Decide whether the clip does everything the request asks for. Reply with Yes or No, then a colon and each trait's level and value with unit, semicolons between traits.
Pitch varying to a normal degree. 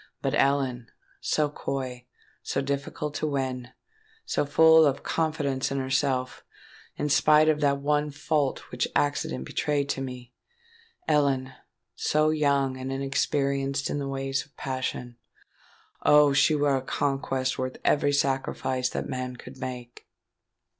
No: narrow, 2.1 semitones